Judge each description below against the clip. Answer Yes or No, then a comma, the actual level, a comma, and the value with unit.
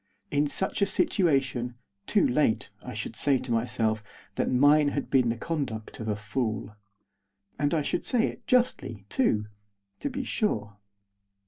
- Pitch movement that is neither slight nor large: No, wide, 6.4 semitones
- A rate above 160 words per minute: No, average, 155 wpm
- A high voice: No, low, 135 Hz